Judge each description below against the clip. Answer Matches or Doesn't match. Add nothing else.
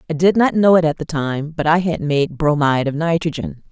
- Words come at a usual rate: Doesn't match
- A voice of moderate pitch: Matches